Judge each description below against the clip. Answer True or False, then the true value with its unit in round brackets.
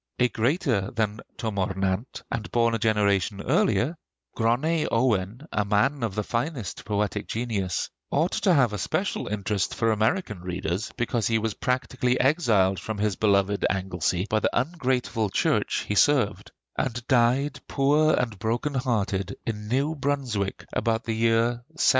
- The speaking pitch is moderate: False (115 Hz)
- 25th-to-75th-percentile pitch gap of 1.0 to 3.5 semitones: False (3.9 semitones)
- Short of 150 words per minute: False (155 wpm)